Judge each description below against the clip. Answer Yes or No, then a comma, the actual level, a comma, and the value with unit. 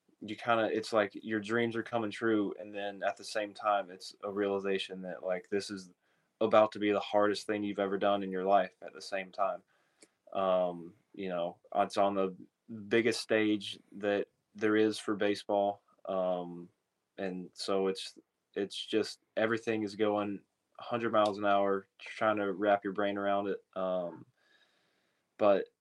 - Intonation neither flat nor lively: No, narrow, 1.7 semitones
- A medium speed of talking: Yes, average, 170 wpm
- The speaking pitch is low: Yes, low, 100 Hz